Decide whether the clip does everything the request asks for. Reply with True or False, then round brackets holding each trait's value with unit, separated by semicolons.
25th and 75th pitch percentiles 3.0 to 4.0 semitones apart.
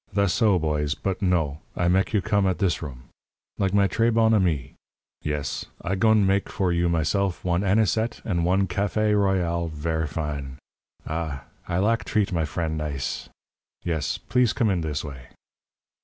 False (4.4 semitones)